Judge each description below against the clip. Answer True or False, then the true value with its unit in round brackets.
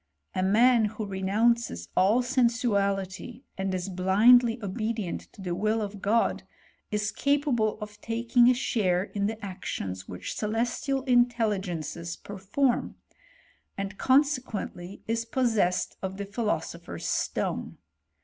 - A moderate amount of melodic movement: True (3.8 semitones)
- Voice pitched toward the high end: True (210 Hz)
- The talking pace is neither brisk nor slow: False (120 wpm)